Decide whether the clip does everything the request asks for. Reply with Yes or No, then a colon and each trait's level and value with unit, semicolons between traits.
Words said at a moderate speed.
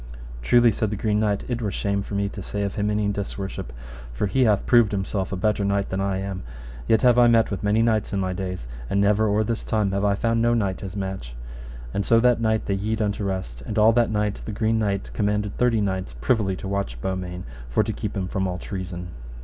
No: fast, 240 wpm